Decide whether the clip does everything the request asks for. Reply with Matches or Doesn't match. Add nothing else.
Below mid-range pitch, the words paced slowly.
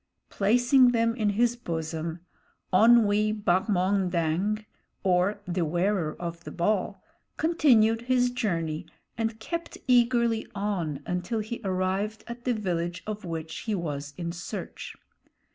Doesn't match